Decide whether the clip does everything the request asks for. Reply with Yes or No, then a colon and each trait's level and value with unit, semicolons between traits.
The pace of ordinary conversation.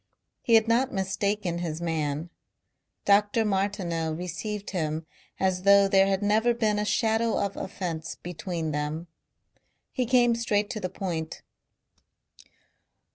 No: slow, 130 wpm